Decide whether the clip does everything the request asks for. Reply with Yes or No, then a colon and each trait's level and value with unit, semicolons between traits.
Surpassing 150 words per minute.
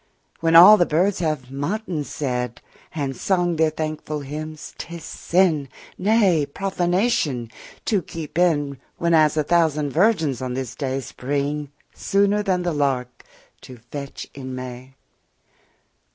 No: slow, 135 wpm